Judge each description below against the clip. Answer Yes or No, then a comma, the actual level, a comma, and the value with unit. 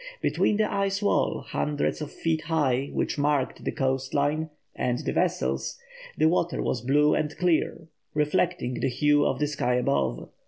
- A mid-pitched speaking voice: Yes, medium, 150 Hz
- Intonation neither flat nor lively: Yes, average, 3.5 semitones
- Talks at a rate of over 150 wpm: Yes, average, 165 wpm